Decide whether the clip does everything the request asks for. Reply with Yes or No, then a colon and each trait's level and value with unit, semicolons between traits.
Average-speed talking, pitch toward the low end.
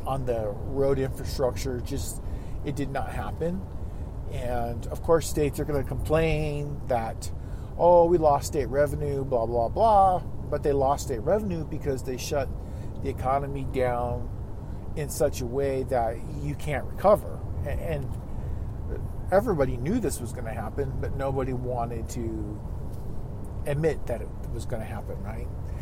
Yes: average, 150 wpm; low, 125 Hz